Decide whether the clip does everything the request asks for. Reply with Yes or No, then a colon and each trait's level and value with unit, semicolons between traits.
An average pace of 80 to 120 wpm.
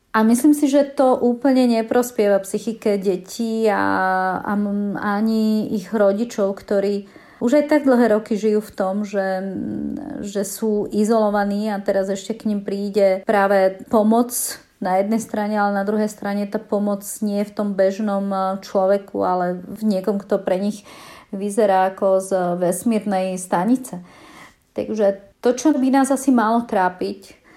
No: average, 150 wpm